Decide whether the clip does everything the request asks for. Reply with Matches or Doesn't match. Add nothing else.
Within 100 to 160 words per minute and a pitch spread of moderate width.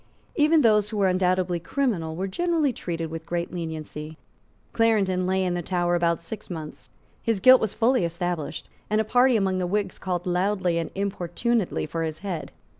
Doesn't match